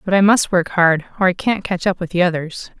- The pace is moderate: No, fast, 280 wpm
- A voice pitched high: No, medium, 180 Hz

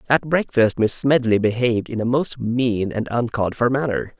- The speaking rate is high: No, average, 185 wpm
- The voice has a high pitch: No, low, 120 Hz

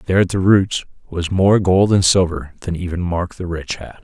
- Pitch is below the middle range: Yes, very low, 90 Hz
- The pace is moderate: No, fast, 225 wpm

